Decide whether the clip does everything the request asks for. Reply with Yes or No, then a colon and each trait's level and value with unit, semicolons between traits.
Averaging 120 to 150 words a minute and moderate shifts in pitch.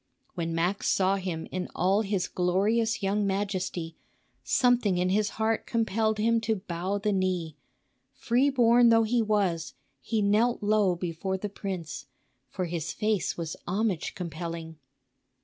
Yes: average, 145 wpm; average, 3.7 semitones